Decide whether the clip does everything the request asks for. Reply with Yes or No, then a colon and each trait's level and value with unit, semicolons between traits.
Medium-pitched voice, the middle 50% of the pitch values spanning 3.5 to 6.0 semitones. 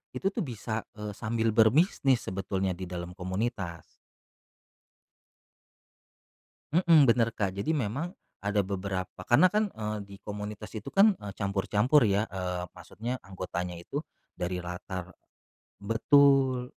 No: low, 105 Hz; average, 5.1 semitones